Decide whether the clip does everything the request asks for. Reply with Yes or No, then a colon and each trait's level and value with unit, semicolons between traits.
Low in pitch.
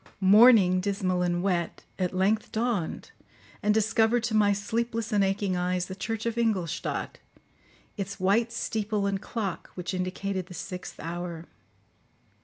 No: high, 200 Hz